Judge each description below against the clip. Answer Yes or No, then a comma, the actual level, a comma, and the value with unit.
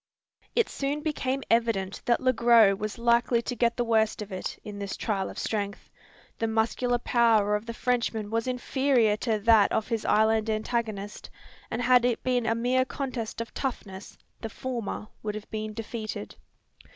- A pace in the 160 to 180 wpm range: Yes, average, 175 wpm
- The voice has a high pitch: Yes, high, 230 Hz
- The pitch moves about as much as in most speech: No, narrow, 2.3 semitones